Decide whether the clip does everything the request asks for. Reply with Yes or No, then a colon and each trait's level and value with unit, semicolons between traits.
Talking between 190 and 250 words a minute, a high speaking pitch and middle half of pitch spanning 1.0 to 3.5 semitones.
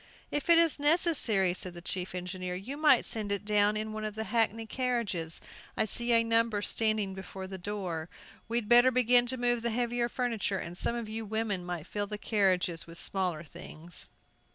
No: average, 195 wpm; high, 215 Hz; average, 4.1 semitones